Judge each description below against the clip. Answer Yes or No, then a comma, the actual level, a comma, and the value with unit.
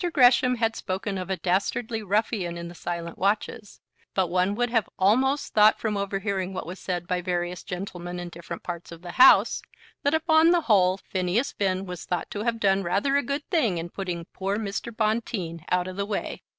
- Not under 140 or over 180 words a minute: No, average, 200 wpm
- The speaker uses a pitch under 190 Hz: No, high, 195 Hz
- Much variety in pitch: No, average, 3.9 semitones